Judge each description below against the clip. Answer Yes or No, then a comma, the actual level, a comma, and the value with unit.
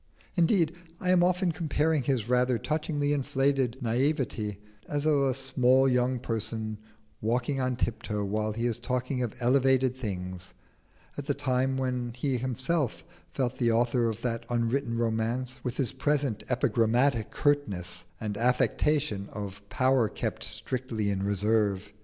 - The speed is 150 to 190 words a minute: No, average, 140 wpm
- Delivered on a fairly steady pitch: No, average, 3.3 semitones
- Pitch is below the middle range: Yes, low, 125 Hz